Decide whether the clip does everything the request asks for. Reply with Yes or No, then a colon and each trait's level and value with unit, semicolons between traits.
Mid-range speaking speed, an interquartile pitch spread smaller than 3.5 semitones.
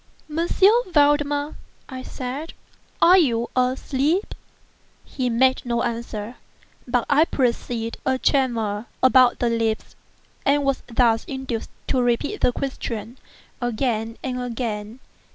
No: slow, 115 wpm; average, 3.0 semitones